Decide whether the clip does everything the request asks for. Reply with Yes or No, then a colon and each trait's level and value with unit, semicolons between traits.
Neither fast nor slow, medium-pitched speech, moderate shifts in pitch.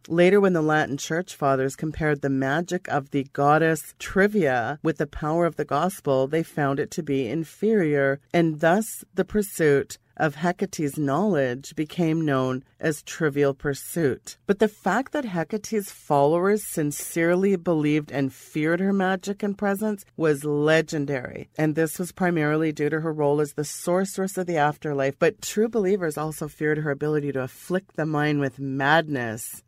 Yes: average, 160 wpm; medium, 155 Hz; average, 3.8 semitones